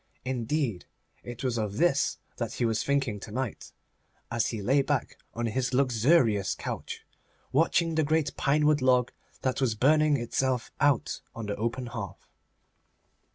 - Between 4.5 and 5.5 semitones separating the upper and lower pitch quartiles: No, average, 3.6 semitones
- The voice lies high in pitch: No, low, 125 Hz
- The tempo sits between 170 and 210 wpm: No, average, 150 wpm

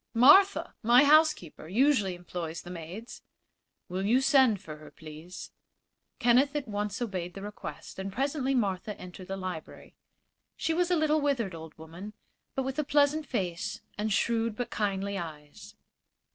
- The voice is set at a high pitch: Yes, high, 210 Hz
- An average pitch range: No, wide, 6.9 semitones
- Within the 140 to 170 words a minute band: Yes, average, 155 wpm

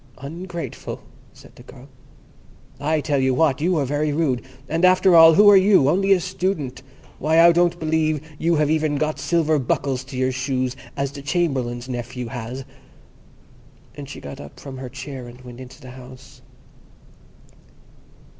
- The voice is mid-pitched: Yes, medium, 145 Hz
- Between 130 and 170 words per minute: Yes, average, 165 wpm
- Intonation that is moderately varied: Yes, average, 4.0 semitones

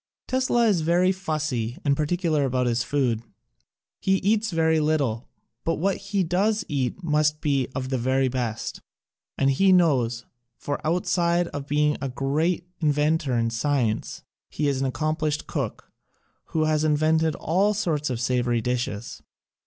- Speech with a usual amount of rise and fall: Yes, average, 4.6 semitones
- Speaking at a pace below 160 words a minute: Yes, average, 150 wpm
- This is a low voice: No, medium, 150 Hz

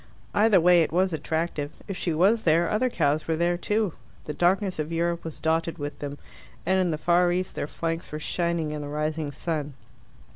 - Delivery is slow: No, fast, 205 wpm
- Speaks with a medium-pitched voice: Yes, medium, 165 Hz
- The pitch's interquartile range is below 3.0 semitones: Yes, narrow, 2.6 semitones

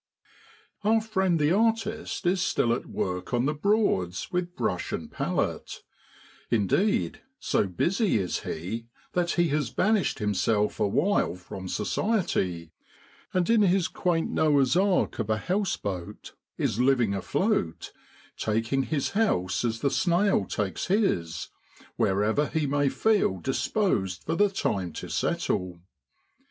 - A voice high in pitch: No, medium, 145 Hz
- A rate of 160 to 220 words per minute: No, slow, 135 wpm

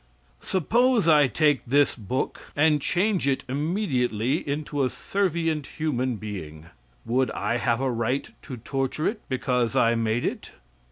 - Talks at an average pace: Yes, average, 145 wpm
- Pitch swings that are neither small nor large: Yes, average, 4.5 semitones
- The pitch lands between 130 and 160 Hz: Yes, low, 135 Hz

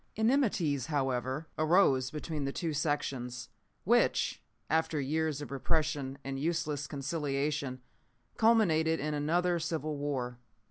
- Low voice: No, medium, 150 Hz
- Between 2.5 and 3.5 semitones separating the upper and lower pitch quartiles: Yes, average, 2.8 semitones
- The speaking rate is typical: No, slow, 110 wpm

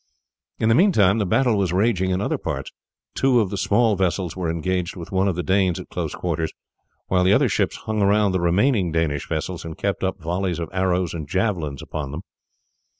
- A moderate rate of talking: No, fast, 210 wpm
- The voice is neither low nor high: No, very low, 95 Hz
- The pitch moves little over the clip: No, average, 3.0 semitones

